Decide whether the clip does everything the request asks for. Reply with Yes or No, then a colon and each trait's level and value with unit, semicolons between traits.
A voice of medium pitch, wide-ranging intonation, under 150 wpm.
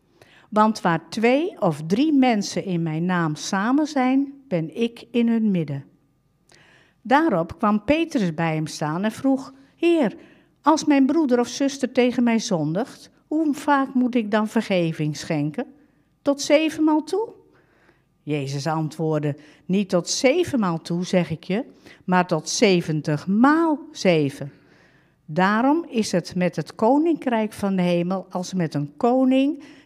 No: high, 210 Hz; wide, 8.6 semitones; average, 140 wpm